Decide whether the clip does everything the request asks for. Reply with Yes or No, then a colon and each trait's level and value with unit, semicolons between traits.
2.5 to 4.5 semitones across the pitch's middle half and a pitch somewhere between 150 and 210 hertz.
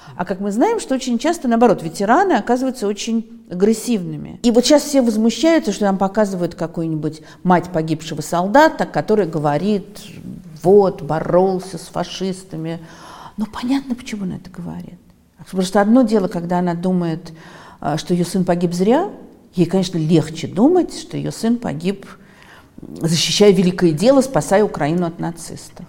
No: average, 5.0 semitones; high, 190 Hz